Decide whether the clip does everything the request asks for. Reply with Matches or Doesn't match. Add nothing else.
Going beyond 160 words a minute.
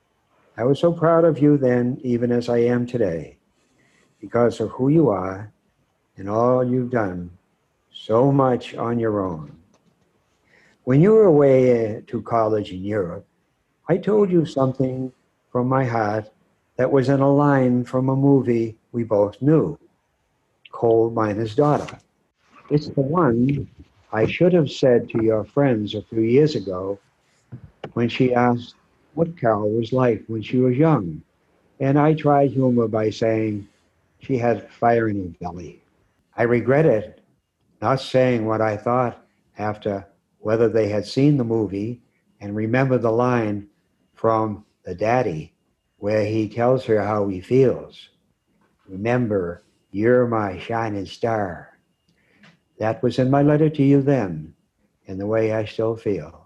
Doesn't match